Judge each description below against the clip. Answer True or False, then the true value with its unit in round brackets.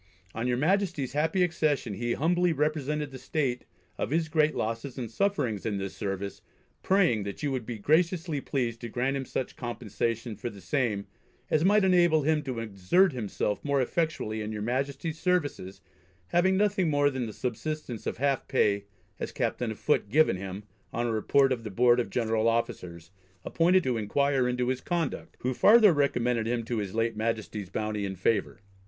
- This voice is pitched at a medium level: False (125 Hz)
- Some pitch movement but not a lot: False (5.8 semitones)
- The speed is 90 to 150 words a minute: False (185 wpm)